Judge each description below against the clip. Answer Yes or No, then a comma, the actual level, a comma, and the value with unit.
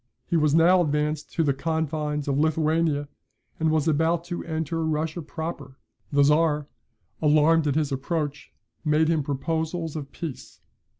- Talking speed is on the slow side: No, average, 145 wpm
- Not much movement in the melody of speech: Yes, narrow, 1.7 semitones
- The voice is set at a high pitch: No, medium, 155 Hz